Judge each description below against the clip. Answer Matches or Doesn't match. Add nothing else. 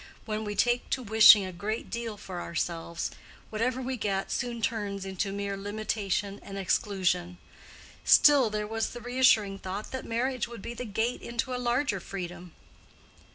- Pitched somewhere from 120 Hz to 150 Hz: Doesn't match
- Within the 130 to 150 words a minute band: Doesn't match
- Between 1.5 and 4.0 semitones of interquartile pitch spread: Matches